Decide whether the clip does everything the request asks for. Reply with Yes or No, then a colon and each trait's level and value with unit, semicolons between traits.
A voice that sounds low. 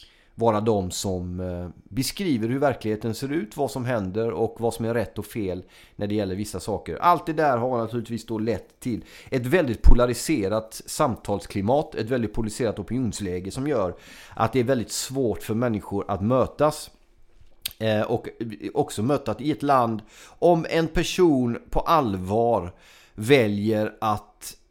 Yes: low, 115 Hz